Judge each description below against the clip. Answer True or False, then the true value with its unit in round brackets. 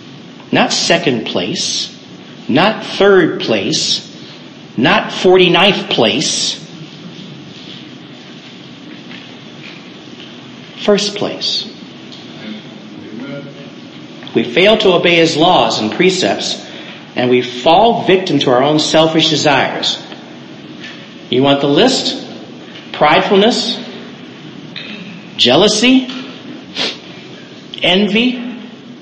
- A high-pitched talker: True (200 Hz)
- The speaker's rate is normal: False (70 wpm)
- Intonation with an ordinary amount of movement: False (6.3 semitones)